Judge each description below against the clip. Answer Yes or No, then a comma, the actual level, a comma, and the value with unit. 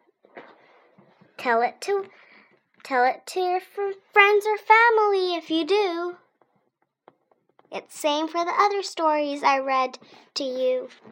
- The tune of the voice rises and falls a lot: No, average, 4.8 semitones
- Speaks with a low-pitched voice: No, very high, 370 Hz